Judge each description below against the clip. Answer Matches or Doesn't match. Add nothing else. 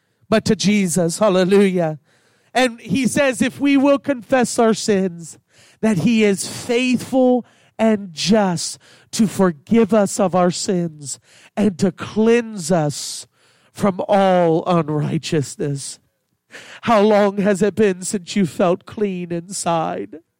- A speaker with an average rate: Doesn't match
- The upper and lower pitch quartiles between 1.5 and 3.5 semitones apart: Doesn't match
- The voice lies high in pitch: Matches